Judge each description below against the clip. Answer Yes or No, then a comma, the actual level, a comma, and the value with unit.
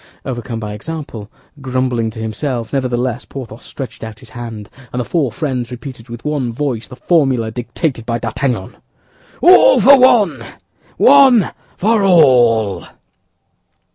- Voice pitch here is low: Yes, low, 125 Hz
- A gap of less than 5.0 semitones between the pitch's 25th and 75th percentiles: Yes, average, 4.5 semitones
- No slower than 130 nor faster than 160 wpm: Yes, slow, 135 wpm